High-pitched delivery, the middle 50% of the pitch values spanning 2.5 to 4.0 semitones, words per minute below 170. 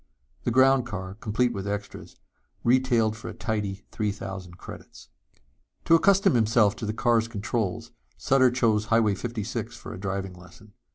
No: low, 110 Hz; average, 3.1 semitones; average, 155 wpm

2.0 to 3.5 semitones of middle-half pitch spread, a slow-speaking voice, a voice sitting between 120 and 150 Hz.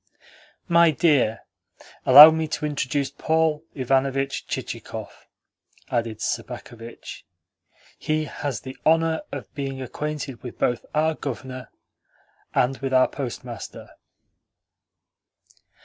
Yes: average, 3.1 semitones; slow, 100 wpm; low, 135 Hz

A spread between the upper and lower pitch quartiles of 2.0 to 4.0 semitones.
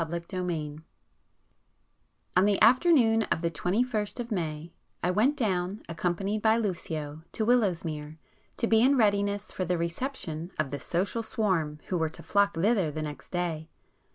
No: average, 5.0 semitones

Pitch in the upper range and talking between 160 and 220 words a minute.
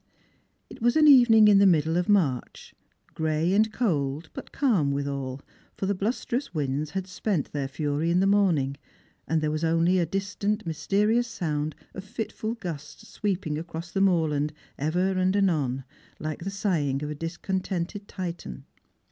No: medium, 175 Hz; average, 165 wpm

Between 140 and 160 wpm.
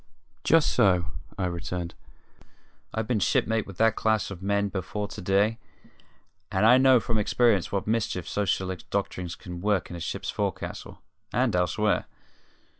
Yes: average, 150 wpm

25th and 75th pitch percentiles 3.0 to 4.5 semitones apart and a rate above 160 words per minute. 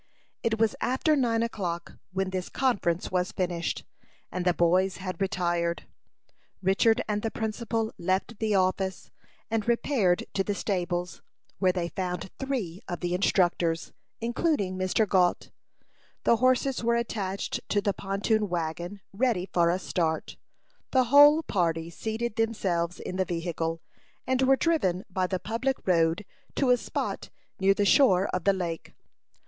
No: average, 4.2 semitones; average, 150 wpm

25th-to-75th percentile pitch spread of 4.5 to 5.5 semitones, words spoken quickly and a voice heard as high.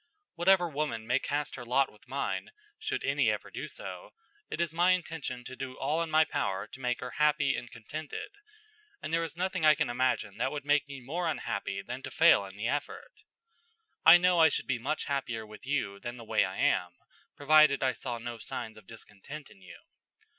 No: average, 4.8 semitones; fast, 210 wpm; medium, 140 Hz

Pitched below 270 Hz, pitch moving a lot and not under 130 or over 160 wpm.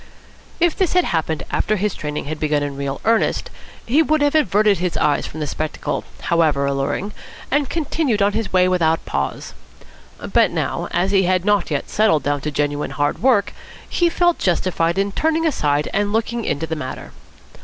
No: medium, 185 Hz; wide, 7.1 semitones; average, 185 wpm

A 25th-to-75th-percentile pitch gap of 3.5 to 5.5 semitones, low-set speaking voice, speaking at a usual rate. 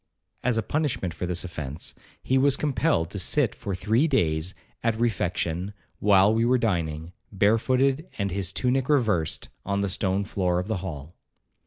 Yes: average, 5.2 semitones; low, 100 Hz; average, 165 wpm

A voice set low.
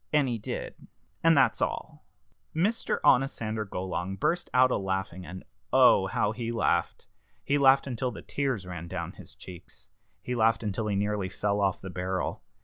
Yes: low, 110 Hz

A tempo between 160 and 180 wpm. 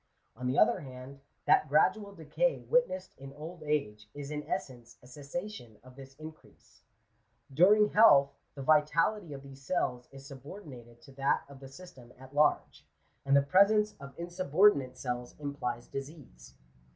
No: average, 150 wpm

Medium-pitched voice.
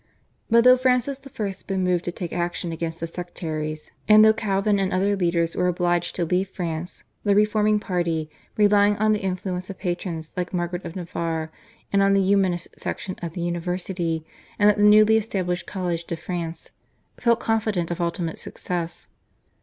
Yes: medium, 180 Hz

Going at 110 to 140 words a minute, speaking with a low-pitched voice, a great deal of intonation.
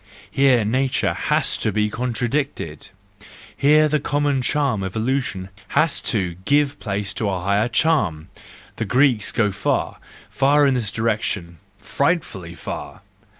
Yes: slow, 135 wpm; low, 115 Hz; wide, 5.9 semitones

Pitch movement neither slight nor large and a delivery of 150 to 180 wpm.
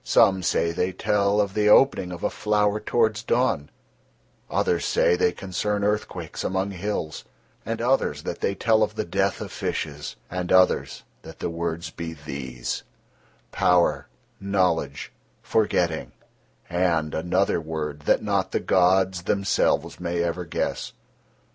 No: average, 3.7 semitones; average, 140 wpm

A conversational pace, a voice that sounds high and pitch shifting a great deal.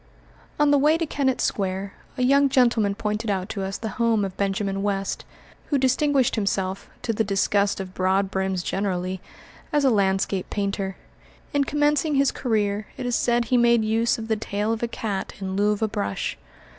No: average, 185 wpm; high, 210 Hz; average, 4.1 semitones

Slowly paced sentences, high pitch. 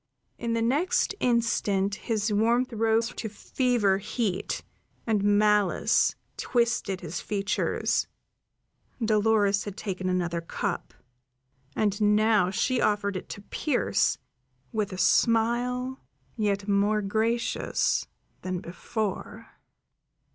Yes: slow, 105 wpm; high, 210 Hz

